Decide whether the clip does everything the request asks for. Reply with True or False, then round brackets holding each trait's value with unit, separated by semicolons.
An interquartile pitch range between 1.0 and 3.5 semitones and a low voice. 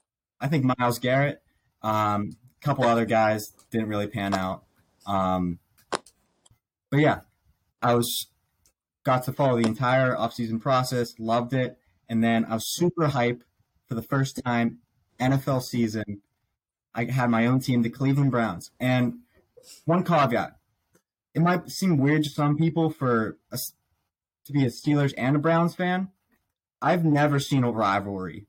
False (4.1 semitones; 120 Hz)